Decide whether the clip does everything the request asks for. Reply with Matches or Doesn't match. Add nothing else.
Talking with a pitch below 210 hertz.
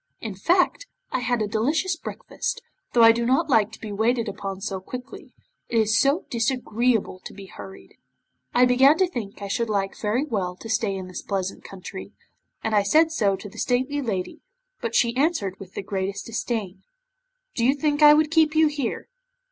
Doesn't match